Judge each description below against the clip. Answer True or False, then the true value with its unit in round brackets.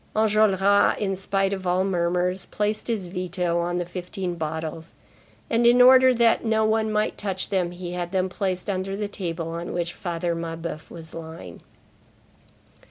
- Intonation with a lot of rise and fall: False (3.0 semitones)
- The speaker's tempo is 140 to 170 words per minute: True (165 wpm)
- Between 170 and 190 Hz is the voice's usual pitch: True (185 Hz)